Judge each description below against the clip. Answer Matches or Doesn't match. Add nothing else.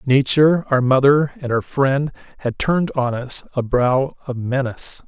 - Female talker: Doesn't match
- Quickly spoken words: Doesn't match